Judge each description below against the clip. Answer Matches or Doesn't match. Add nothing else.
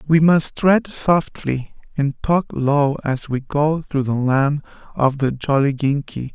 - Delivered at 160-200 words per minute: Doesn't match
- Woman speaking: Doesn't match